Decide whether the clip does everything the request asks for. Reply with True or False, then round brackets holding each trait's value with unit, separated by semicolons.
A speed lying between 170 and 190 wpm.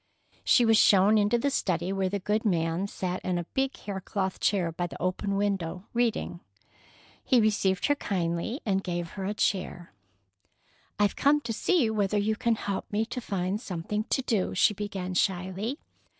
True (180 wpm)